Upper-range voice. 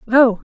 Yes: high, 245 Hz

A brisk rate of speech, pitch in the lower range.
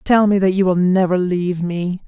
No: fast, 230 wpm; medium, 185 Hz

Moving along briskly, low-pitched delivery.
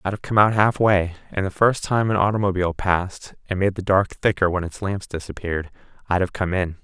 Yes: fast, 220 wpm; very low, 95 Hz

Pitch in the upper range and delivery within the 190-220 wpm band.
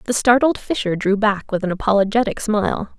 No: high, 210 Hz; average, 180 wpm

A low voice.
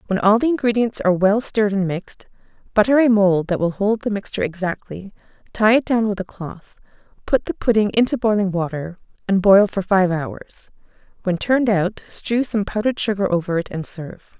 No: high, 200 Hz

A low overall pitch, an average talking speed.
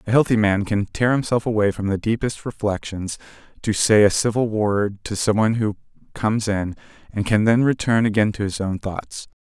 Yes: low, 105 Hz; average, 190 wpm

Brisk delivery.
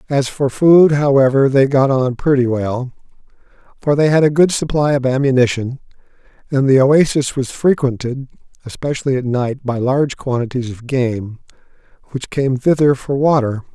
No: average, 155 wpm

